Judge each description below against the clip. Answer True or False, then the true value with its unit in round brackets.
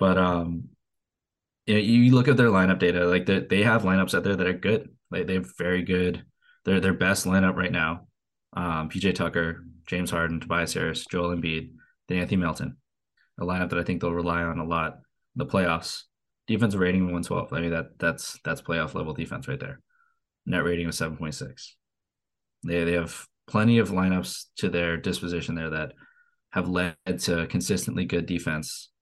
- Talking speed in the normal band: True (185 wpm)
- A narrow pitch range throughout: True (2.0 semitones)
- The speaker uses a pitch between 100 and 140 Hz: False (90 Hz)